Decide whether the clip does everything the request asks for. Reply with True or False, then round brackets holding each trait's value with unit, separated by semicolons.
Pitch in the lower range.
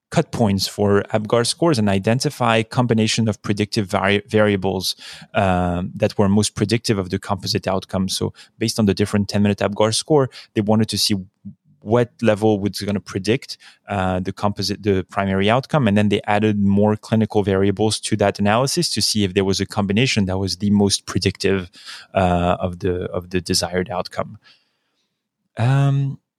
True (105 Hz)